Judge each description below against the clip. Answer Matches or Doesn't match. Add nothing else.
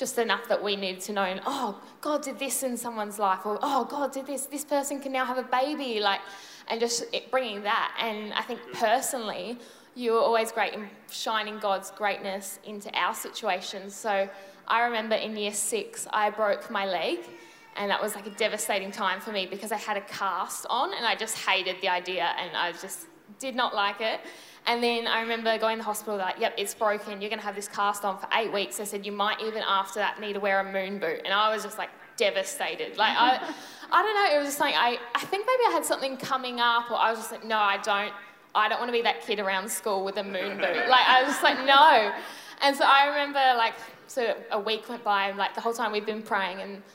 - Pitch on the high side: Matches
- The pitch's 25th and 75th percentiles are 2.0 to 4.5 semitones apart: Matches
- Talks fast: Matches